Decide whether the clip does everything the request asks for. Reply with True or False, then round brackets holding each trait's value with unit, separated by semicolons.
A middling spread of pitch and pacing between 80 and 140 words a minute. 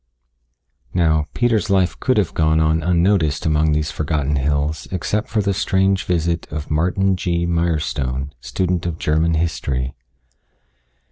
True (3.3 semitones; 135 wpm)